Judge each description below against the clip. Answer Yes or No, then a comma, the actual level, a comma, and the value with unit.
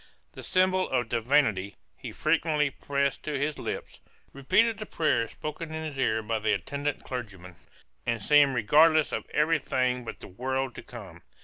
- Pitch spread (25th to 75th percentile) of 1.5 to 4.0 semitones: No, average, 4.6 semitones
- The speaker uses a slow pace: No, average, 170 wpm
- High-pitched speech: No, medium, 140 Hz